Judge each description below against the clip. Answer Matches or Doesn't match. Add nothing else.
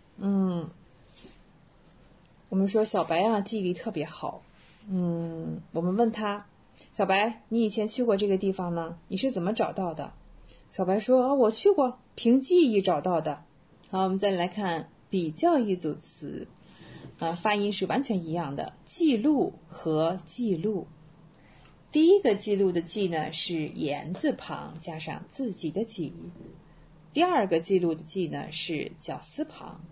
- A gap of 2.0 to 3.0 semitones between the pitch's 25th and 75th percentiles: Doesn't match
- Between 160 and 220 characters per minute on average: Matches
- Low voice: Doesn't match